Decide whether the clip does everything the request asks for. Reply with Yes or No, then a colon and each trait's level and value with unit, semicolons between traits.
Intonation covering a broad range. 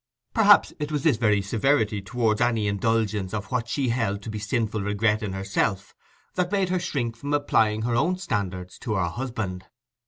No: average, 4.1 semitones